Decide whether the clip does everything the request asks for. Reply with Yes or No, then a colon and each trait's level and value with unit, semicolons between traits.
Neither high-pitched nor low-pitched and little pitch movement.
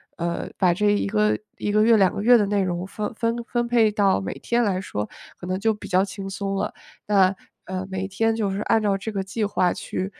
No: high, 200 Hz; narrow, 2.3 semitones